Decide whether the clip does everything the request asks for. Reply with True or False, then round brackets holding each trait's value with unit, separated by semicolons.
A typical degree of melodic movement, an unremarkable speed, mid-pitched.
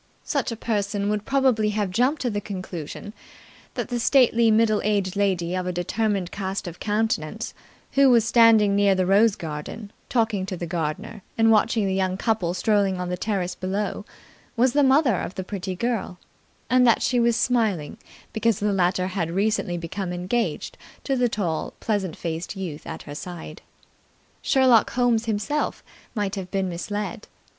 False (3.8 semitones; 165 wpm; 205 Hz)